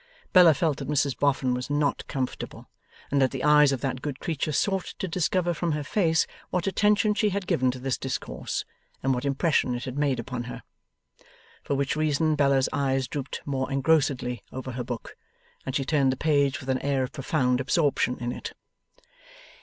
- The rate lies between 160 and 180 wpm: No, average, 190 wpm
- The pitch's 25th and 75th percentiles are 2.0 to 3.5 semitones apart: Yes, average, 3.1 semitones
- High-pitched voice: No, medium, 140 Hz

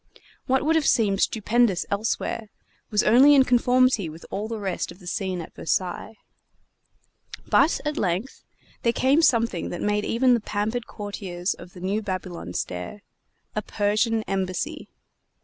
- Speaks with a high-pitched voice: Yes, high, 210 Hz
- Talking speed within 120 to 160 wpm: Yes, average, 150 wpm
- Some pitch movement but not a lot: Yes, average, 4.4 semitones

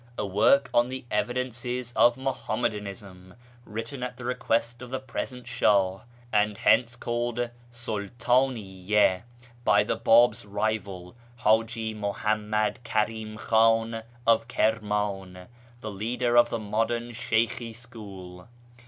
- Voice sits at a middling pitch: No, low, 115 Hz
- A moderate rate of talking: No, slow, 115 wpm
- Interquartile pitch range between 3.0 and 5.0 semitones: No, narrow, 2.6 semitones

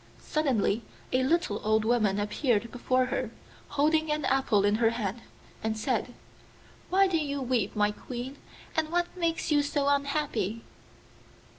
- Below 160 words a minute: Yes, average, 145 wpm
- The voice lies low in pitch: No, very high, 255 Hz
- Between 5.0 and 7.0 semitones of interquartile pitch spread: Yes, average, 5.3 semitones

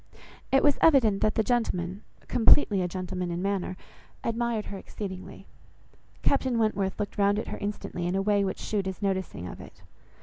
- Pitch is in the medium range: No, high, 200 Hz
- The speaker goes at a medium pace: Yes, average, 175 wpm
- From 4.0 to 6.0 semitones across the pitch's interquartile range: No, average, 2.9 semitones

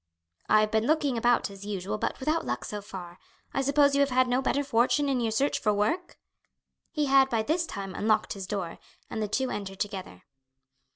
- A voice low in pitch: No, high, 225 Hz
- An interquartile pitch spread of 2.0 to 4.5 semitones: No, average, 5.2 semitones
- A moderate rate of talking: No, fast, 210 wpm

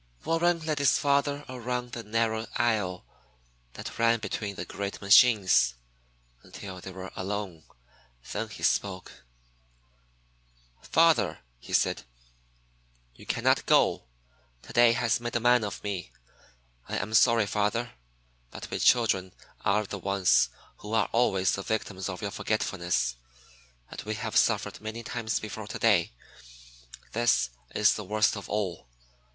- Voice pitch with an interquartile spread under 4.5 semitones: Yes, average, 3.4 semitones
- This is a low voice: Yes, low, 105 Hz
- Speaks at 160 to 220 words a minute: No, slow, 135 wpm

